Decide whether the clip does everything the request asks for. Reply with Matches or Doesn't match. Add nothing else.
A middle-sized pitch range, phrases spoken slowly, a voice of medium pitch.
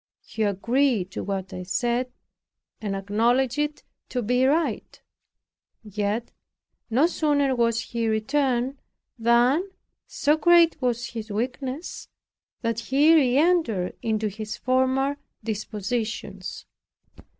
Doesn't match